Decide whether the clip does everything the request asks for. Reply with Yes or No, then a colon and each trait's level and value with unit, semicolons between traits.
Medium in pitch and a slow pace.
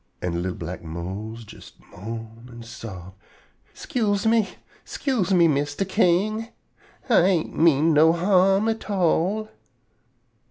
Yes: medium, 165 Hz; slow, 120 wpm